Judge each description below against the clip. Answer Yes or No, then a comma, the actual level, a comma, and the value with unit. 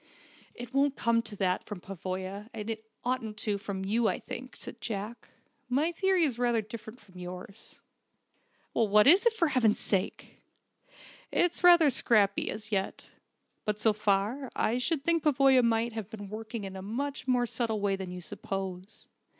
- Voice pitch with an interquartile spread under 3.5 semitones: No, average, 4.2 semitones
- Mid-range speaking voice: No, high, 220 Hz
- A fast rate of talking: No, average, 165 wpm